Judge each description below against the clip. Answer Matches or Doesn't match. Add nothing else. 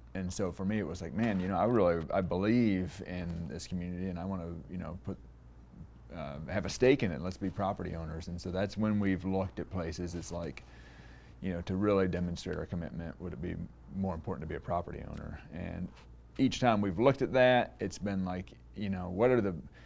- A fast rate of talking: Matches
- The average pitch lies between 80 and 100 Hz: Matches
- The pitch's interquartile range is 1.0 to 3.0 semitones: Matches